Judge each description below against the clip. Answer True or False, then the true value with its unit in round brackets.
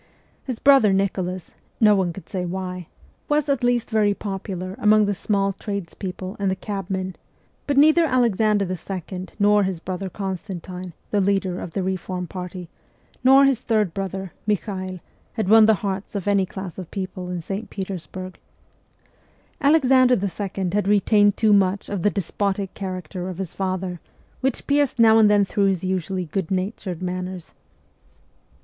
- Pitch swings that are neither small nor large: False (2.2 semitones)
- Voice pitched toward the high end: True (195 Hz)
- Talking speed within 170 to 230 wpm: False (160 wpm)